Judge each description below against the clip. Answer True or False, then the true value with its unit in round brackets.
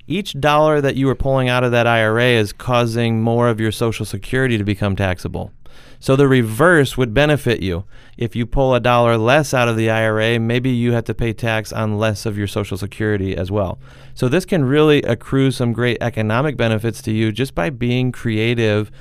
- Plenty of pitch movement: False (2.9 semitones)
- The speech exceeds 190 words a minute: True (205 wpm)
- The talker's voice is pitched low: True (120 Hz)